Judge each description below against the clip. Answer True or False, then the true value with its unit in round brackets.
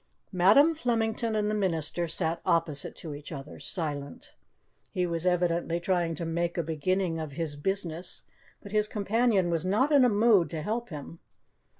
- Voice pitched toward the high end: False (175 Hz)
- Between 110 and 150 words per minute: False (170 wpm)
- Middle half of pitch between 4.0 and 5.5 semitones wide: True (4.3 semitones)